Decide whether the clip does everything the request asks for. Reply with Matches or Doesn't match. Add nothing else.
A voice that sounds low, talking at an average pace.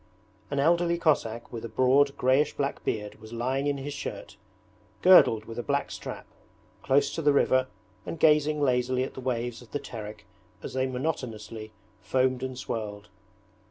Matches